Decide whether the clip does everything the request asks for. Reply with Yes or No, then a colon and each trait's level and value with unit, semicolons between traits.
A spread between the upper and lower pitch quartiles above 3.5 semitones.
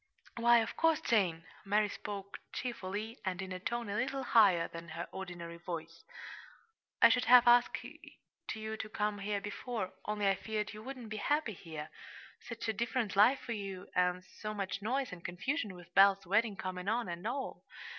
Yes: average, 4.0 semitones